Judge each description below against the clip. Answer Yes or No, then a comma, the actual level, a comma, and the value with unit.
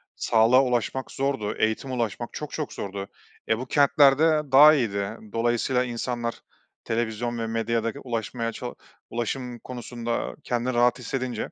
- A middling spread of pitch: No, narrow, 2.1 semitones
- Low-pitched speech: Yes, low, 120 Hz